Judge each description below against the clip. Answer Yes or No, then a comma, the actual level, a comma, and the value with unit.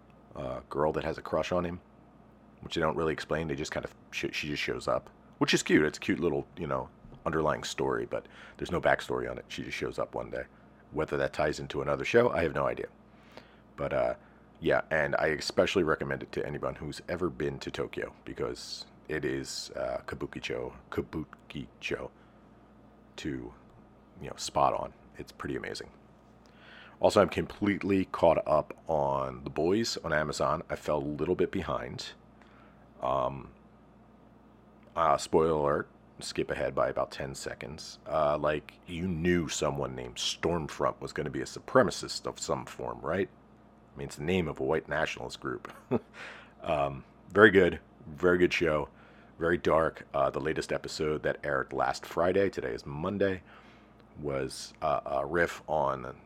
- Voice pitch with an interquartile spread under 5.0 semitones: Yes, average, 4.4 semitones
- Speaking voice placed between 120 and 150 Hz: No, very low, 75 Hz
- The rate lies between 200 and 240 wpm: No, average, 175 wpm